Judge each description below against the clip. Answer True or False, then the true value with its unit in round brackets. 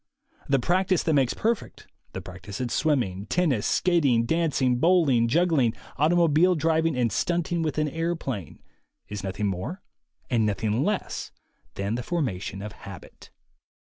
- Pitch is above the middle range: False (140 Hz)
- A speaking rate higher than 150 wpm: False (135 wpm)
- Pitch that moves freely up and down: True (7.3 semitones)